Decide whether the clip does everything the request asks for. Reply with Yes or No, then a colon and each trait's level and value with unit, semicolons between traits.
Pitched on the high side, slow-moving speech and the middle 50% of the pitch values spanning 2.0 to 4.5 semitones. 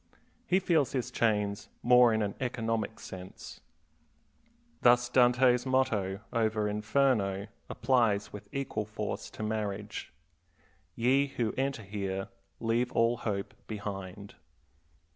No: low, 110 Hz; slow, 110 wpm; average, 3.2 semitones